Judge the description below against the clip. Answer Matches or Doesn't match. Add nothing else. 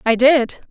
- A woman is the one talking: Matches